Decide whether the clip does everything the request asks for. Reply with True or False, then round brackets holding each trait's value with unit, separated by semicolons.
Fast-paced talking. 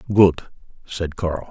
False (120 wpm)